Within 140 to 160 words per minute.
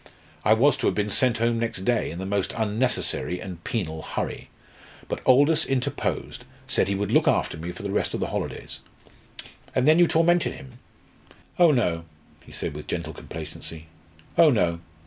No: average, 180 wpm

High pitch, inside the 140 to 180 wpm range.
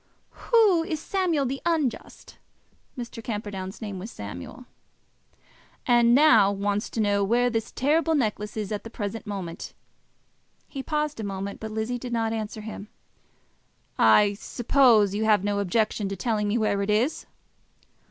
Yes: high, 220 Hz; average, 150 wpm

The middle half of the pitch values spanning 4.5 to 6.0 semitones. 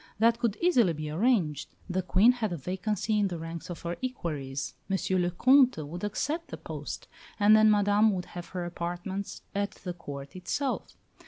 No: average, 4.1 semitones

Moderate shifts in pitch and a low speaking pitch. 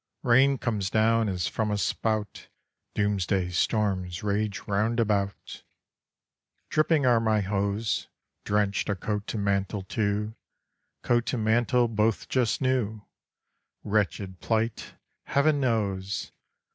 No: narrow, 2.3 semitones; low, 105 Hz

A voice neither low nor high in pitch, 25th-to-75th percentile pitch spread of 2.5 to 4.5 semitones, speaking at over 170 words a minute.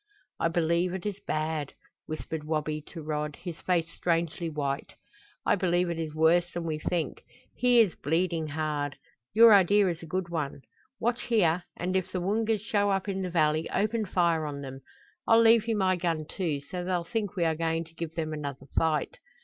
Yes: medium, 170 Hz; average, 3.3 semitones; average, 195 wpm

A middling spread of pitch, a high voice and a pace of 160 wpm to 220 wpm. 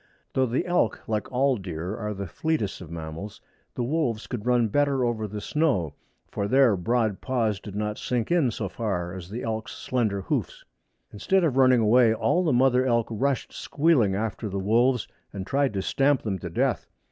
No: average, 4.4 semitones; low, 115 Hz; average, 190 wpm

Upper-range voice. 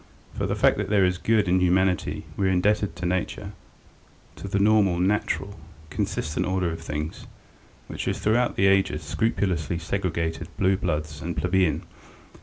No: very low, 90 Hz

